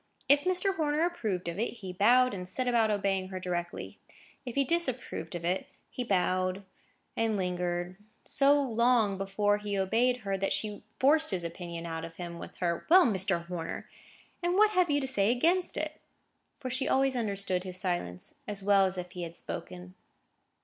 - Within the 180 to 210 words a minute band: Yes, average, 185 wpm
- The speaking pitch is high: Yes, high, 200 Hz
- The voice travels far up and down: Yes, wide, 5.9 semitones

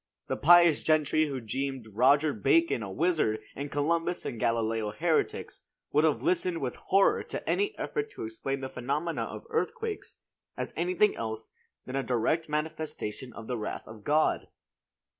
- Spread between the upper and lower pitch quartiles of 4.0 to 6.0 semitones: Yes, wide, 5.6 semitones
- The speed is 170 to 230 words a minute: No, average, 160 wpm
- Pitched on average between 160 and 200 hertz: No, medium, 145 Hz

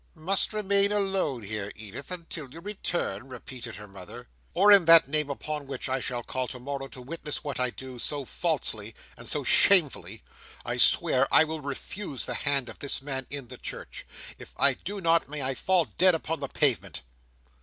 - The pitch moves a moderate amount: Yes, average, 4.8 semitones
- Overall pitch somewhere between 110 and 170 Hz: Yes, medium, 140 Hz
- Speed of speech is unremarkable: Yes, average, 190 wpm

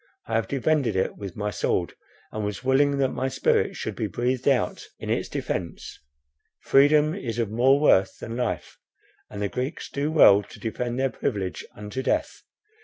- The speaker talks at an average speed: Yes, average, 180 wpm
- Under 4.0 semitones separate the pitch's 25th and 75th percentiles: No, average, 4.7 semitones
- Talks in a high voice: No, low, 120 Hz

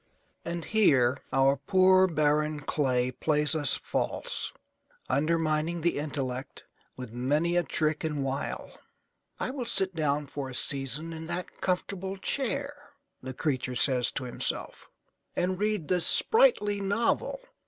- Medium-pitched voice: Yes, medium, 155 Hz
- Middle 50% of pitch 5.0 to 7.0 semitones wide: Yes, average, 5.3 semitones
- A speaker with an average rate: No, slow, 130 wpm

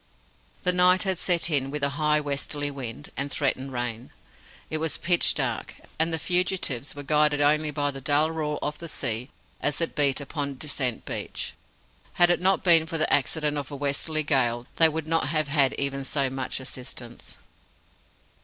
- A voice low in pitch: No, medium, 145 Hz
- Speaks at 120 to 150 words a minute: No, average, 180 wpm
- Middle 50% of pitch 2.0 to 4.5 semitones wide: Yes, average, 2.8 semitones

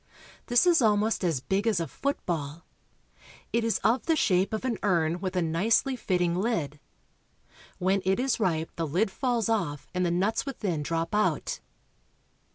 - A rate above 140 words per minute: Yes, average, 165 wpm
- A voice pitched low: No, high, 190 Hz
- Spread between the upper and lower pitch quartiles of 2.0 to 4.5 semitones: No, average, 5.1 semitones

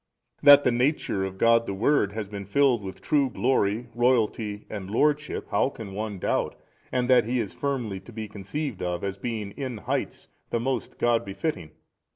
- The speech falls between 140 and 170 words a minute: No, average, 190 wpm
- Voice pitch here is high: No, low, 115 Hz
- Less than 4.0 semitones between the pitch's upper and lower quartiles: No, average, 4.4 semitones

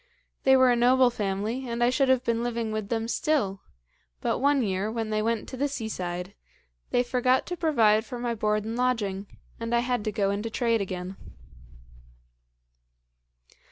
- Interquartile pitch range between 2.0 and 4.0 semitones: Yes, average, 3.0 semitones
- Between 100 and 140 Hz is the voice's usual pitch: No, high, 230 Hz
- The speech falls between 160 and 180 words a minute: Yes, average, 175 wpm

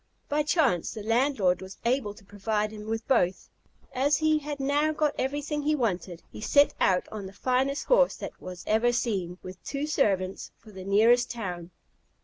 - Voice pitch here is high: Yes, high, 230 Hz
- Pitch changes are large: Yes, wide, 6.6 semitones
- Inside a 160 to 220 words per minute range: Yes, average, 180 wpm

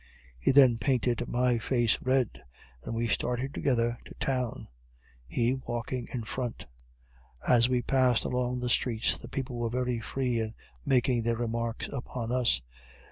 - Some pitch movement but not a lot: No, narrow, 1.5 semitones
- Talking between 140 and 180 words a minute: Yes, average, 150 wpm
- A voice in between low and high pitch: No, low, 120 Hz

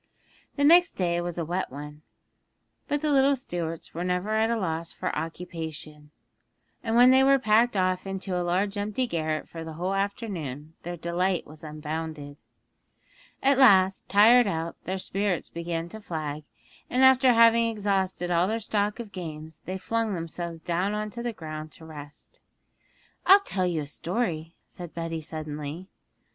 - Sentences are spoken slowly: No, average, 165 wpm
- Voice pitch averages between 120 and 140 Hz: No, medium, 180 Hz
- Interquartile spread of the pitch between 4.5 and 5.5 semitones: Yes, average, 5.1 semitones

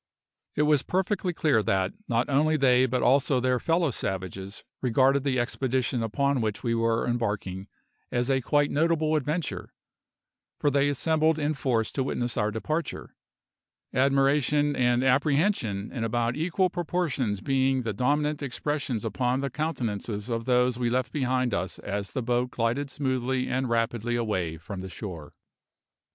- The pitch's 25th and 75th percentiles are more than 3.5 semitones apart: Yes, average, 4.0 semitones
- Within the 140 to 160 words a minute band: Yes, average, 150 wpm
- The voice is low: Yes, low, 130 Hz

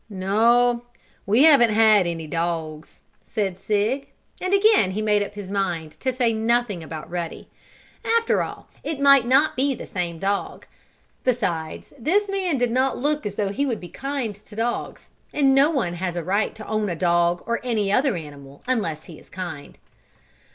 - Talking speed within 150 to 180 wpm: Yes, average, 175 wpm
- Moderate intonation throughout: No, wide, 6.6 semitones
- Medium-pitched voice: No, high, 215 Hz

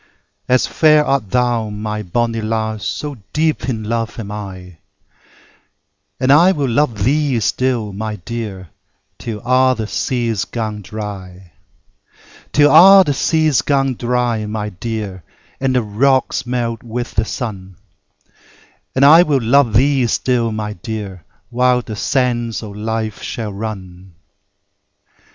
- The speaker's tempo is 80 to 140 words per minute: Yes, slow, 135 wpm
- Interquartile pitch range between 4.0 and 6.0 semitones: No, average, 3.6 semitones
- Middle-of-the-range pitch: No, low, 115 Hz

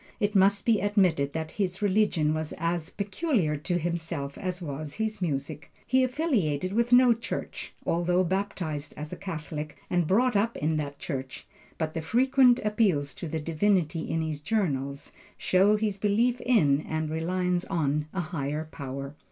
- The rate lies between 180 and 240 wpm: No, average, 160 wpm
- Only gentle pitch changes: No, average, 5.1 semitones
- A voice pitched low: No, medium, 175 Hz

